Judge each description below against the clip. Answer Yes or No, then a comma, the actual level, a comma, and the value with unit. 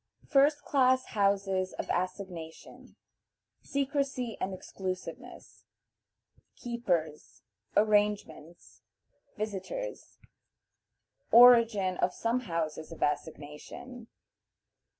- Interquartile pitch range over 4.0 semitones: Yes, wide, 5.6 semitones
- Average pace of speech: No, slow, 70 wpm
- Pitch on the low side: No, high, 200 Hz